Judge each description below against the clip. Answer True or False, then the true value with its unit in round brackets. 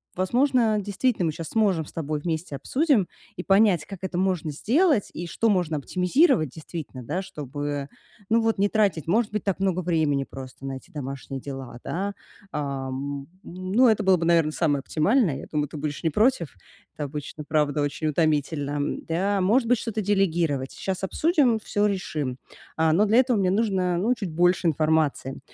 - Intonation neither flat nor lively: False (5.7 semitones)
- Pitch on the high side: False (170 Hz)